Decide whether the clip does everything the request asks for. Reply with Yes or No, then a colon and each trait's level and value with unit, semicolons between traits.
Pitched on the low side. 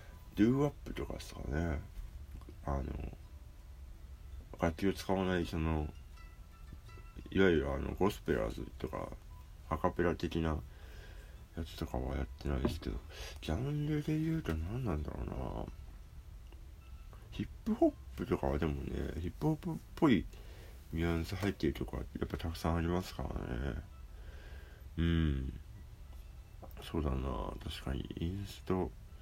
Yes: very low, 80 Hz